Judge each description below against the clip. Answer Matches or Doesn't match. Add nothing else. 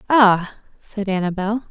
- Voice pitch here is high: Matches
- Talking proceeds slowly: Matches